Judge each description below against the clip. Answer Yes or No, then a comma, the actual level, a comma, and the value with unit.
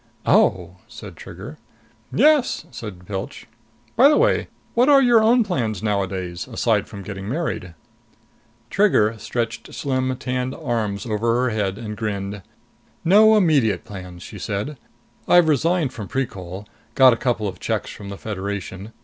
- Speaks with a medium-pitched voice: No, low, 115 Hz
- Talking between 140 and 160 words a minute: Yes, average, 145 wpm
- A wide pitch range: Yes, wide, 7.0 semitones